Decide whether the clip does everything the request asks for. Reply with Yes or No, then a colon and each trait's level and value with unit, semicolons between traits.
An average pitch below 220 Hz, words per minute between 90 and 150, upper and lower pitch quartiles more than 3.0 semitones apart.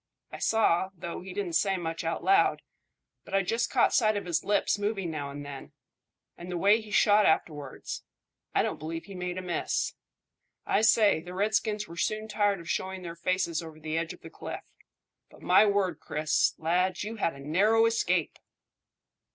No: medium, 185 Hz; average, 190 wpm; average, 4.0 semitones